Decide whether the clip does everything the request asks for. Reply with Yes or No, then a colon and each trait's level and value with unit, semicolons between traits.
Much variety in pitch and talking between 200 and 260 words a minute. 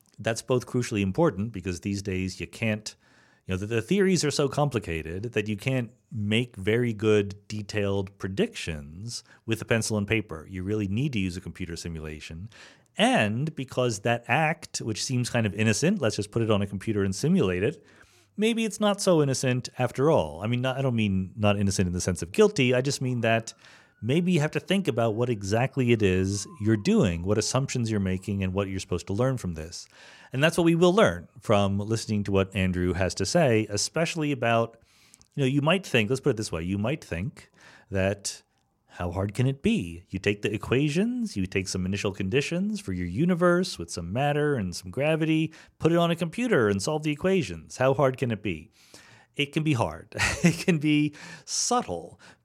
Yes: wide, 6.3 semitones; fast, 205 wpm